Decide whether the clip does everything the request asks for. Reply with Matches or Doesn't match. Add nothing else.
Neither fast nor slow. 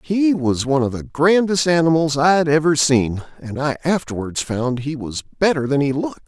Matches